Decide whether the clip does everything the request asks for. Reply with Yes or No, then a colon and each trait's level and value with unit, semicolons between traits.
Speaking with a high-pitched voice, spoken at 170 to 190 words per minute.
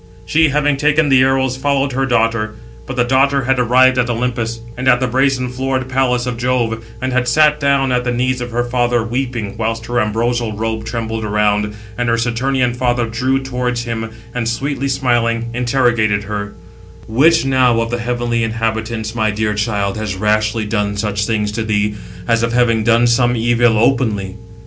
No: low, 120 Hz; average, 185 wpm